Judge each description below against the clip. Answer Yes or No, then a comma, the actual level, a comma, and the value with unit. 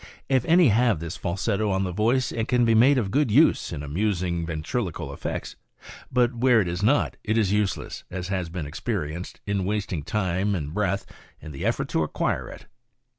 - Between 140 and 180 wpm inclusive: No, average, 190 wpm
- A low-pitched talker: Yes, low, 100 Hz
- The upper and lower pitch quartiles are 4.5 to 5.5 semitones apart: Yes, average, 5.0 semitones